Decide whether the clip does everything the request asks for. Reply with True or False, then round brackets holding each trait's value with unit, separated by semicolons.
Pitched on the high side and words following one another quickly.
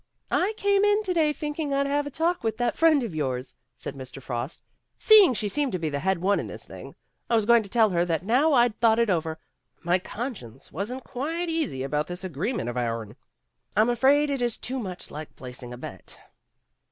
True (225 Hz; 225 wpm)